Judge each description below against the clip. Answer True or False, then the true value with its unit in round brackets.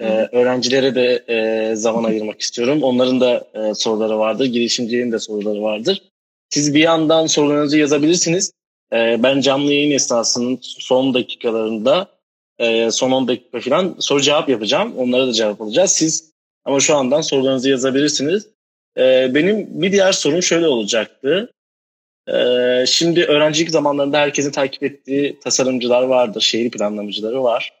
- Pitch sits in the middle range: False (130 Hz)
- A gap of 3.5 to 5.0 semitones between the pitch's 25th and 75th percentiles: True (4.4 semitones)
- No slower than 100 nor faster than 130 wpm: False (140 wpm)